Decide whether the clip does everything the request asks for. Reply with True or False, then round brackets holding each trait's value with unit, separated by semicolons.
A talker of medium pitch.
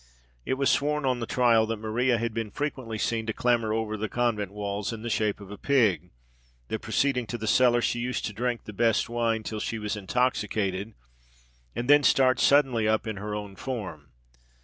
False (115 Hz)